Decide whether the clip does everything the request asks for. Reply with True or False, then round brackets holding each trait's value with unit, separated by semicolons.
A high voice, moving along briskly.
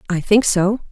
False (200 Hz; 195 wpm)